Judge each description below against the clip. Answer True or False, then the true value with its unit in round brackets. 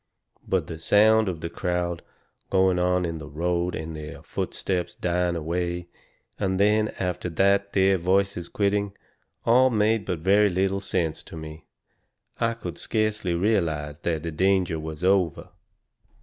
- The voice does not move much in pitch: False (3.0 semitones)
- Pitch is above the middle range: False (90 Hz)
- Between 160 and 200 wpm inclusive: False (145 wpm)